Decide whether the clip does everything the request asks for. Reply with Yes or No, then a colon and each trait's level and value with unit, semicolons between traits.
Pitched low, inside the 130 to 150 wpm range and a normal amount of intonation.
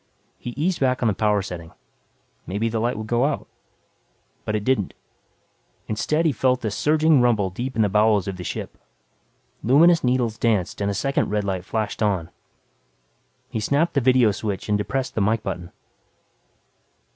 No: low, 110 Hz; average, 170 wpm; average, 4.0 semitones